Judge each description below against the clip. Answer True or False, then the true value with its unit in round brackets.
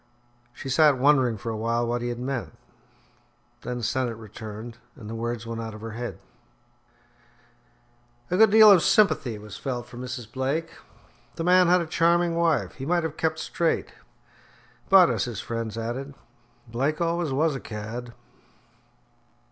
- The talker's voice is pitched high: False (125 Hz)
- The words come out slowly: False (160 wpm)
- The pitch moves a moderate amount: False (5.9 semitones)